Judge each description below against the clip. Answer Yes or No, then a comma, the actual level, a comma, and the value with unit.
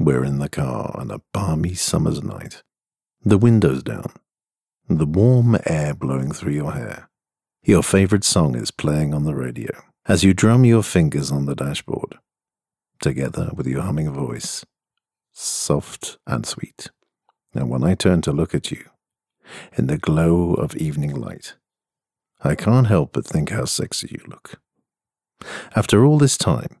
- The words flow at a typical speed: Yes, average, 160 wpm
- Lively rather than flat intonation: Yes, wide, 6.1 semitones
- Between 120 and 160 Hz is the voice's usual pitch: No, very low, 85 Hz